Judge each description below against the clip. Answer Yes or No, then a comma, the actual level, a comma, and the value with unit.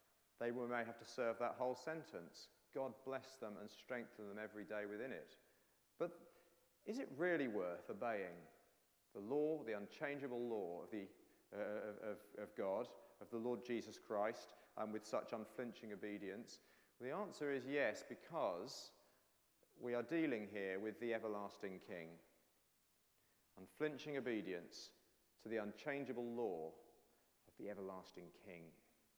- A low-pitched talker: Yes, low, 115 Hz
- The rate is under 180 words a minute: Yes, average, 140 wpm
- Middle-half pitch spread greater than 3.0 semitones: Yes, average, 4.2 semitones